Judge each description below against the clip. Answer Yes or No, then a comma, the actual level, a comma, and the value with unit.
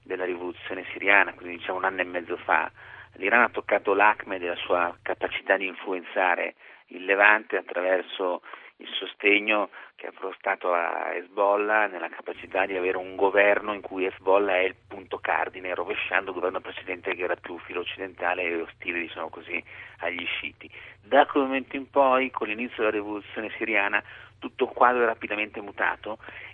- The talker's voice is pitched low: Yes, low, 100 Hz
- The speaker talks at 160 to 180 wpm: Yes, average, 165 wpm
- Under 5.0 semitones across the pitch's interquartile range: Yes, average, 2.7 semitones